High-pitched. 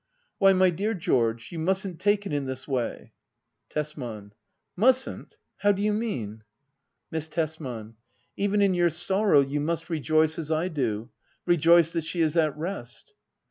No: medium, 160 Hz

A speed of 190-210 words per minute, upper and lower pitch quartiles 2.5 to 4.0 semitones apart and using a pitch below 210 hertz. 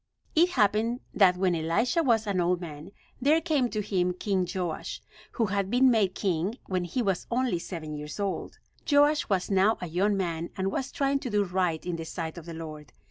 No: fast, 205 wpm; average, 5.1 semitones; high, 190 Hz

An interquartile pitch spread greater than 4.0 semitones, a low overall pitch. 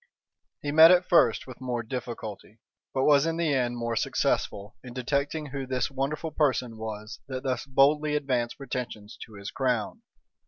No: average, 3.5 semitones; low, 130 Hz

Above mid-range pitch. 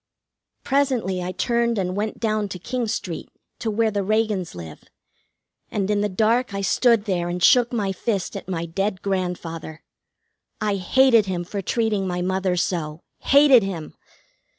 Yes: high, 200 Hz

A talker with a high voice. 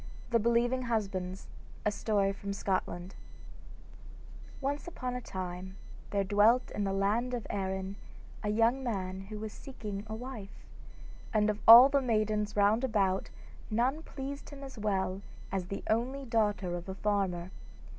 Yes: high, 210 Hz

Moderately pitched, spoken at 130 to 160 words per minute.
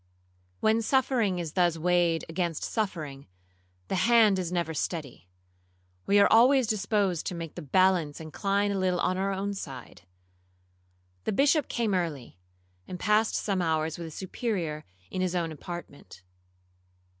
Yes: medium, 180 Hz; average, 145 wpm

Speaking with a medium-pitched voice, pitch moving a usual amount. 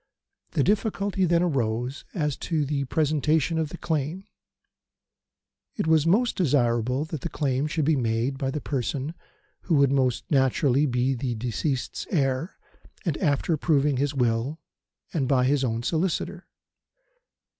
Yes: medium, 145 Hz; average, 3.7 semitones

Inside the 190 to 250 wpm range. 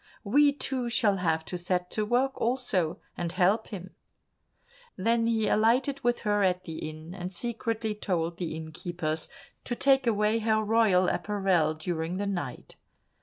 No: average, 155 wpm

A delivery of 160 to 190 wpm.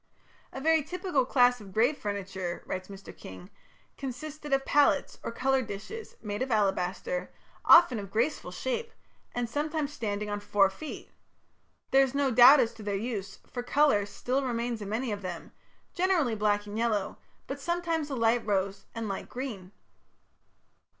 Yes: average, 165 wpm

